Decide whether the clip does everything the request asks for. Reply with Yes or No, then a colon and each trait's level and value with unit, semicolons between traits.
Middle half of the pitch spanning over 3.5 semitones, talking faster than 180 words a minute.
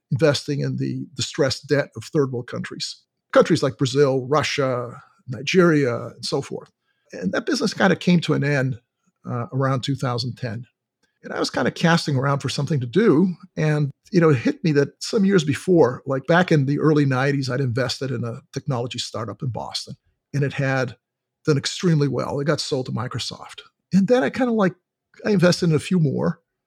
Yes: average, 4.1 semitones; average, 195 wpm